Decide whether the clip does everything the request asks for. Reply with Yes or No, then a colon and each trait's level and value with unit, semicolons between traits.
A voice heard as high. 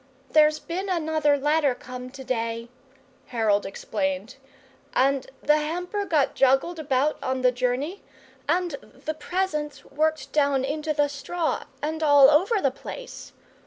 Yes: very high, 295 Hz